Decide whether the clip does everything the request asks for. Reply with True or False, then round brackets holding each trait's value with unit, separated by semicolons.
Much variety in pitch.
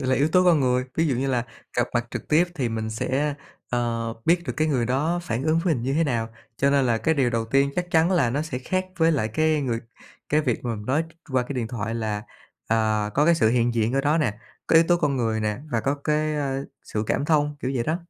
False (4.8 semitones)